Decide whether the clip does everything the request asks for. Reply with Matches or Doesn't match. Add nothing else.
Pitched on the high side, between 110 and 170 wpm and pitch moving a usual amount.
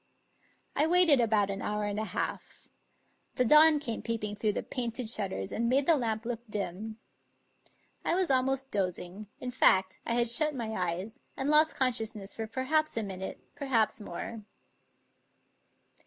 Matches